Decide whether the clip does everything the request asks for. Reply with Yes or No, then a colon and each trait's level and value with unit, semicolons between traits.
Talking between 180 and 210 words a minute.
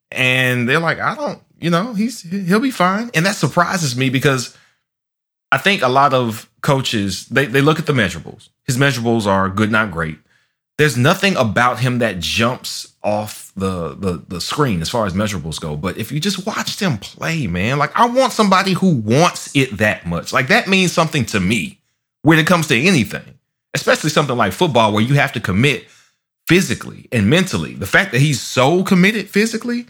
Yes: average, 195 wpm